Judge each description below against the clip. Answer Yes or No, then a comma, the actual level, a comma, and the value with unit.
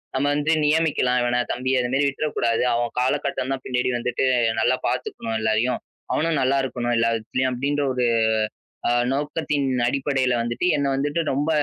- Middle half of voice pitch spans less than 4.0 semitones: Yes, average, 2.9 semitones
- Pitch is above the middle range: No, low, 130 Hz